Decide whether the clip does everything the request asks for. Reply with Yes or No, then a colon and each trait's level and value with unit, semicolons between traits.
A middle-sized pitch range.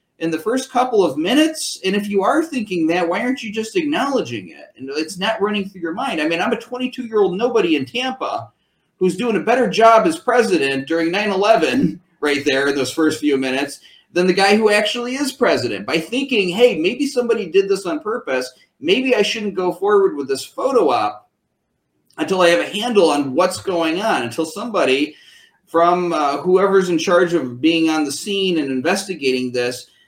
No: wide, 7.0 semitones